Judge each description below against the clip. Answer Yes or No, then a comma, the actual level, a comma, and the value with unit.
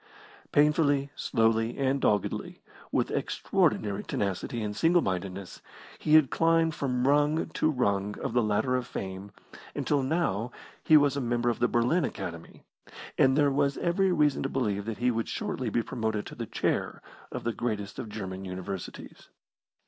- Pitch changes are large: Yes, wide, 5.7 semitones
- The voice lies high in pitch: No, low, 120 Hz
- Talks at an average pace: Yes, average, 160 wpm